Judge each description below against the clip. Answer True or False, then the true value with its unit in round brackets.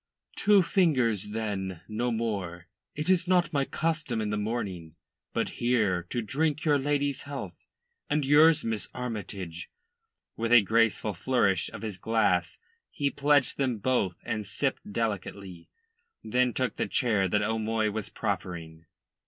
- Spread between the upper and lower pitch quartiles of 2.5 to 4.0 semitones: False (5.6 semitones)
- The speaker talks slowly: False (145 wpm)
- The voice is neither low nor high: False (115 Hz)